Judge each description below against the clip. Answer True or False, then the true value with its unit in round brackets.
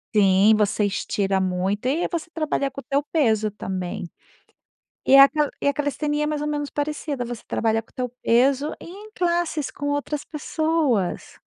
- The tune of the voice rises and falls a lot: True (6.0 semitones)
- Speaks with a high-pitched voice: True (280 Hz)